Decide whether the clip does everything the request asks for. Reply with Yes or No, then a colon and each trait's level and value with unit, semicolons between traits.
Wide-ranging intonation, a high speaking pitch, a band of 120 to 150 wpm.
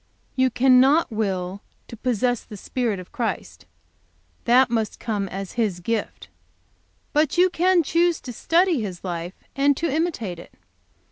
Yes: wide, 6.6 semitones; high, 240 Hz; average, 145 wpm